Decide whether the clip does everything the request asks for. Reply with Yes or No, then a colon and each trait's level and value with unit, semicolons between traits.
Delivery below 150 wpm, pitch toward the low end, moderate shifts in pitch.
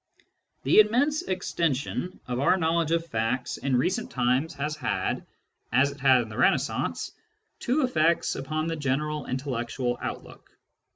No: average, 140 wpm; medium, 150 Hz; average, 4.6 semitones